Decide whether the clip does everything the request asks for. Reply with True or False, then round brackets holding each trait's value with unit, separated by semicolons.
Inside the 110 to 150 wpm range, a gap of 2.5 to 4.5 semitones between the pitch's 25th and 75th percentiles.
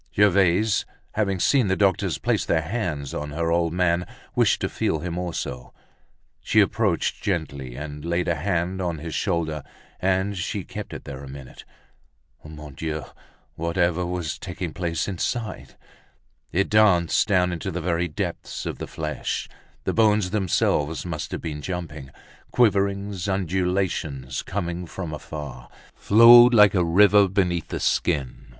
True (145 wpm; 3.8 semitones)